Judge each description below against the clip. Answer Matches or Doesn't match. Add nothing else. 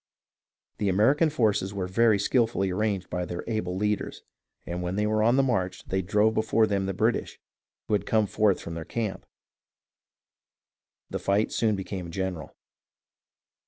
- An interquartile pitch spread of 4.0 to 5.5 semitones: Doesn't match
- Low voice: Matches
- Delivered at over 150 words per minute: Matches